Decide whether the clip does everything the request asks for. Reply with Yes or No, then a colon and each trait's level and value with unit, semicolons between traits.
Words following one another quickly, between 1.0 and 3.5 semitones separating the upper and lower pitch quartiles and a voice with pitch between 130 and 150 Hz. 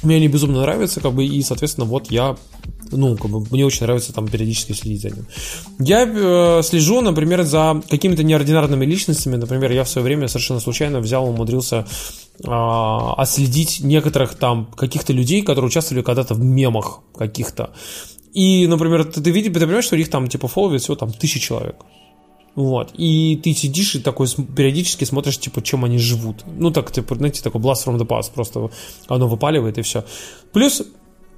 No: fast, 175 wpm; average, 4.7 semitones; low, 135 Hz